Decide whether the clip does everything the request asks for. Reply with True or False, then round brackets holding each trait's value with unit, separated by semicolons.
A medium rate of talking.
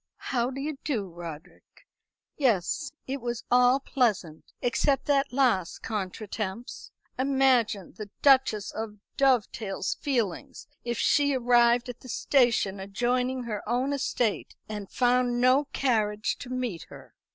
False (130 wpm)